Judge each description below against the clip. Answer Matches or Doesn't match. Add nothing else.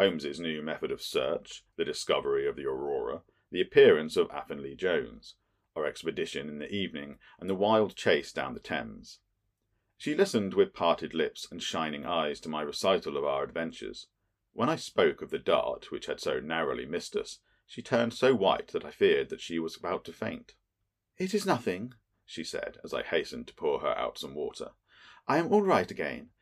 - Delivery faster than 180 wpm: Matches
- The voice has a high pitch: Matches